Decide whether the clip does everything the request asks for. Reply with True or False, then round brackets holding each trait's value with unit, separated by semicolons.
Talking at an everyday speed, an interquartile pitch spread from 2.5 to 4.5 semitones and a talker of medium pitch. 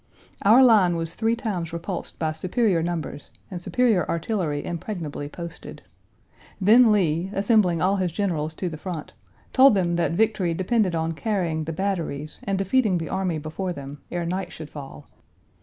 True (160 wpm; 3.7 semitones; 175 Hz)